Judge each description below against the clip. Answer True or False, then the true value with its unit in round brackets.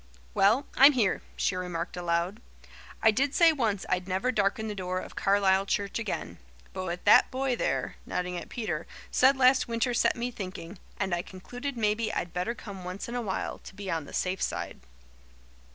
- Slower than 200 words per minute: True (190 wpm)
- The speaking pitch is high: True (200 Hz)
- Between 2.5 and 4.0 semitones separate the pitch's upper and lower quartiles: False (4.7 semitones)